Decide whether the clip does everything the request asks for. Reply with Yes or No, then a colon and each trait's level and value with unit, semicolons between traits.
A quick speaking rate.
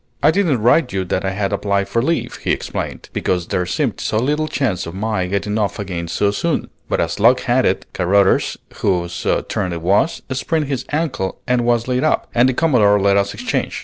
Yes: fast, 210 wpm